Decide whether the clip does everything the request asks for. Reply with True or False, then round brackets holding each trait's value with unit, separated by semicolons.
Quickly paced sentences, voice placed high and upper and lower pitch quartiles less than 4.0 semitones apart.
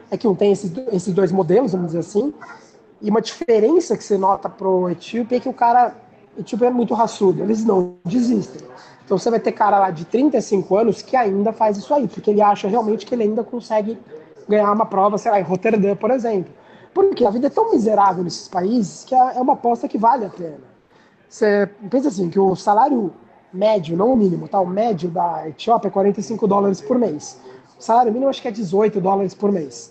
True (215 wpm; 210 Hz; 3.3 semitones)